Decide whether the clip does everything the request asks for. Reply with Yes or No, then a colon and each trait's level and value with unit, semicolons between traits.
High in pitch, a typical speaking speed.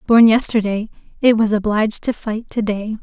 Yes: high, 220 Hz; average, 180 wpm